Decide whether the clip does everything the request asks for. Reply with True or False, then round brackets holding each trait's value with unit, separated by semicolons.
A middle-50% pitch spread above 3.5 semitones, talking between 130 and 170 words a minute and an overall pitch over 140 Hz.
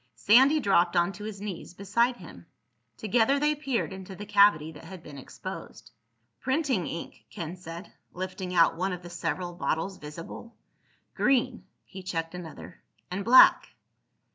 True (4.6 semitones; 145 wpm; 190 Hz)